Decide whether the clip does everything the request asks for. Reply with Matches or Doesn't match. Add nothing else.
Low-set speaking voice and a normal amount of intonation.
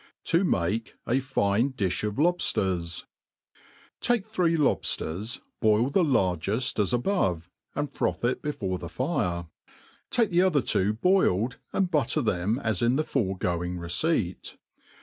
Doesn't match